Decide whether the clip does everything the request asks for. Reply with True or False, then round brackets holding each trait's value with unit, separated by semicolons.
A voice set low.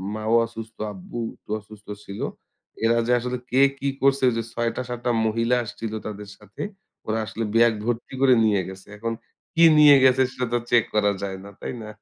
True (115 Hz)